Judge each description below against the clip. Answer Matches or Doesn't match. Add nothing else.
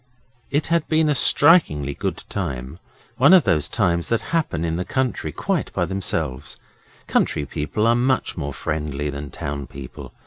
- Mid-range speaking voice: Doesn't match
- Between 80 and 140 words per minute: Doesn't match